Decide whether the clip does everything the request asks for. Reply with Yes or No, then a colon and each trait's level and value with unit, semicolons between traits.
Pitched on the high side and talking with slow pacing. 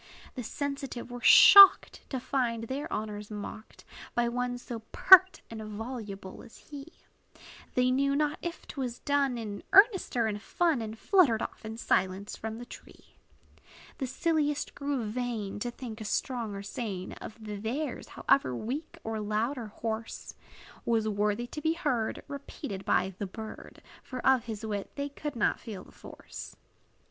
No: high, 235 Hz; average, 165 wpm